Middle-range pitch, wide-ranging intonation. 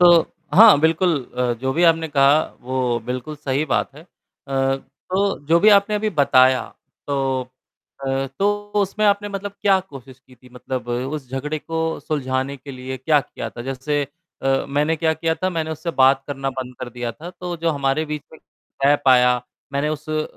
No: medium, 145 Hz; average, 3.8 semitones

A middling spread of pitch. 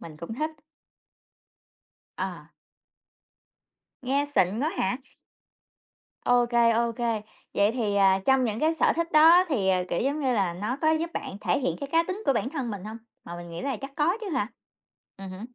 No: wide, 6.6 semitones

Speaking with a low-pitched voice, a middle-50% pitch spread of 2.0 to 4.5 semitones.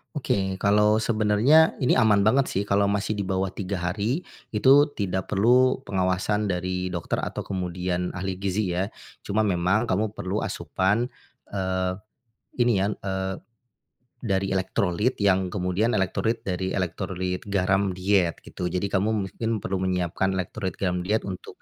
Yes: very low, 95 Hz; narrow, 2.4 semitones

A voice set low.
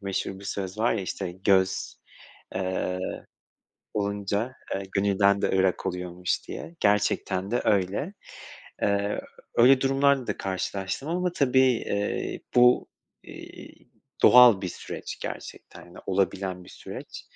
Yes: low, 100 Hz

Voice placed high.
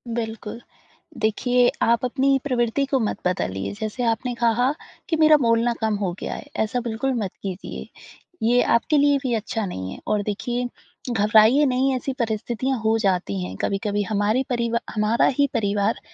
Yes: high, 230 Hz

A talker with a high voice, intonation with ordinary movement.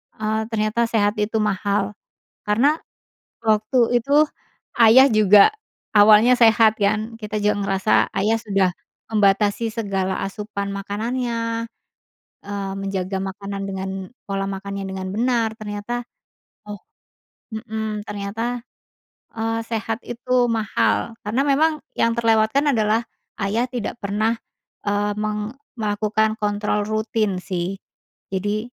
No: high, 215 Hz; narrow, 2.2 semitones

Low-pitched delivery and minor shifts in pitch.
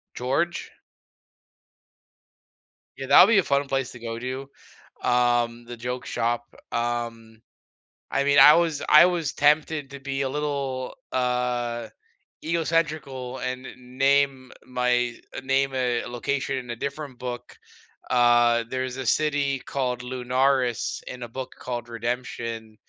Yes: low, 130 Hz; narrow, 2.3 semitones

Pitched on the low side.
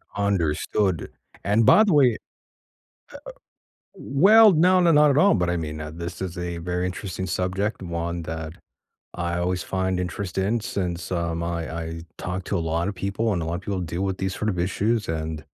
Yes: very low, 90 Hz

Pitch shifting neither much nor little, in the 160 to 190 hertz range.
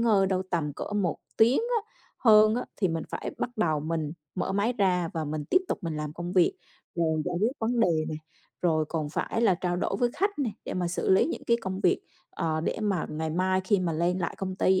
Yes: average, 4.7 semitones; medium, 185 Hz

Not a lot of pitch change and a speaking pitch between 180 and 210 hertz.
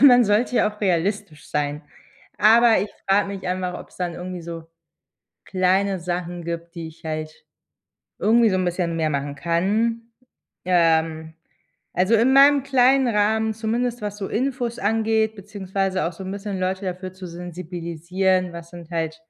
No: average, 4.3 semitones; medium, 185 Hz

